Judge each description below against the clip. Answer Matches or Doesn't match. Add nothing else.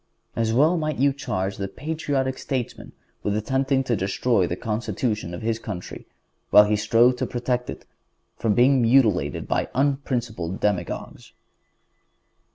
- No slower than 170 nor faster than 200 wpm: Doesn't match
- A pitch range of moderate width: Matches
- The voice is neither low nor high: Doesn't match